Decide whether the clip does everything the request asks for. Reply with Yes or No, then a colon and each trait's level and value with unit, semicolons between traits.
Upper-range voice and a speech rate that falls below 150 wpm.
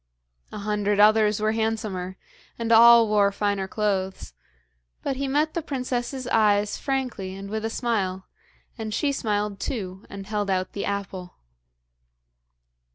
Yes: high, 210 Hz; average, 140 wpm